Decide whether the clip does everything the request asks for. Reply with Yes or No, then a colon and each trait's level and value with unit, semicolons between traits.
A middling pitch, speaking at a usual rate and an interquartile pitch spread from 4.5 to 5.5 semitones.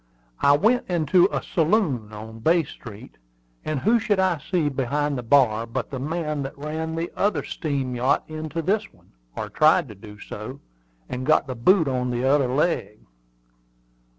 Yes: medium, 145 Hz; average, 170 wpm; average, 4.9 semitones